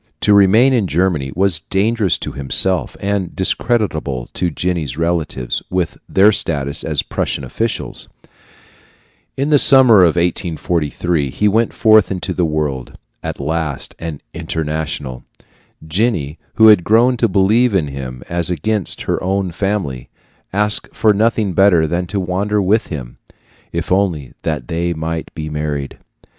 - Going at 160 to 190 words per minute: No, average, 140 wpm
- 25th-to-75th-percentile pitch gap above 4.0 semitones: Yes, average, 4.9 semitones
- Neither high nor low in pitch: No, very low, 90 Hz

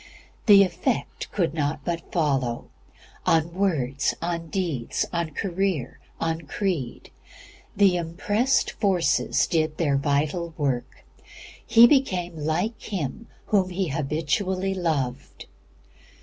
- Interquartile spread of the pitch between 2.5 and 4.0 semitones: No, average, 4.4 semitones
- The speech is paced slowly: Yes, slow, 105 wpm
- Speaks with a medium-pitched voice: Yes, medium, 170 Hz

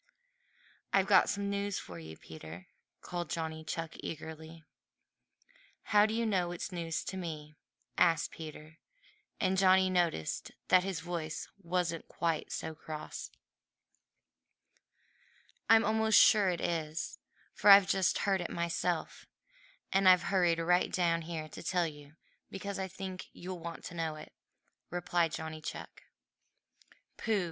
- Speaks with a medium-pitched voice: Yes, medium, 175 Hz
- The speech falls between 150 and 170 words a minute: No, slow, 135 wpm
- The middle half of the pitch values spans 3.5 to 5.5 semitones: No, average, 3.0 semitones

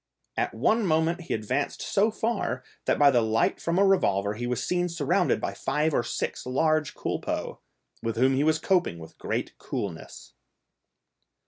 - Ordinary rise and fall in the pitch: No, wide, 7.1 semitones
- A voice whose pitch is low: No, medium, 150 Hz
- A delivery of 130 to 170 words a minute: Yes, average, 165 wpm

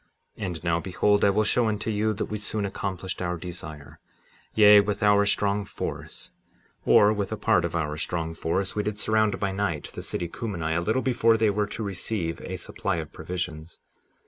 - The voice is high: No, low, 100 Hz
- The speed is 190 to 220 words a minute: Yes, average, 200 wpm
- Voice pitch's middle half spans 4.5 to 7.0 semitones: No, average, 3.6 semitones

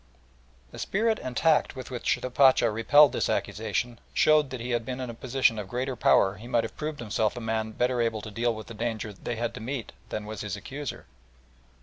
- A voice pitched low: Yes, low, 120 Hz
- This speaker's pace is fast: Yes, fast, 225 wpm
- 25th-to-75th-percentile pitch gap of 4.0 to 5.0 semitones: No, average, 2.8 semitones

